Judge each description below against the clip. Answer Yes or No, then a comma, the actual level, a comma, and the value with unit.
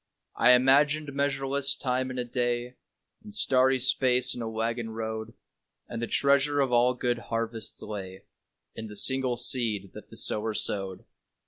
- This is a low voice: Yes, low, 125 Hz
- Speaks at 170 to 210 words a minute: No, average, 155 wpm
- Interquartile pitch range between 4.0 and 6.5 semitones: No, average, 3.0 semitones